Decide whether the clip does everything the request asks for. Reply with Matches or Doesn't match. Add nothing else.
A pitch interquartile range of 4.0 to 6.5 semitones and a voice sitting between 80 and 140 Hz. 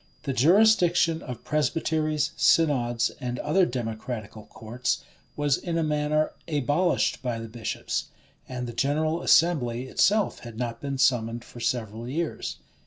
Matches